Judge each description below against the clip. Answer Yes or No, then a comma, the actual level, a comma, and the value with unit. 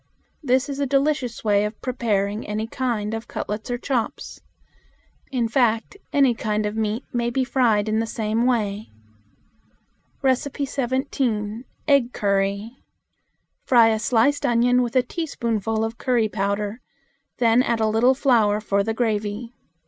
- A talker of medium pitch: No, high, 230 Hz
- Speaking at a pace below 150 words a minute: Yes, average, 140 wpm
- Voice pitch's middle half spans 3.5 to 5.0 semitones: No, average, 3.0 semitones